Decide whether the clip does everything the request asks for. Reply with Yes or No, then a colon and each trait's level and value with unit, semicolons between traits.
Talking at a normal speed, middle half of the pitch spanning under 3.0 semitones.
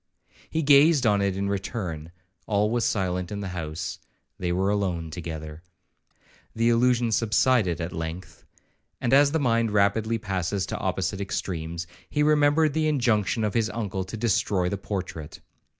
No: average, 150 wpm; average, 4.6 semitones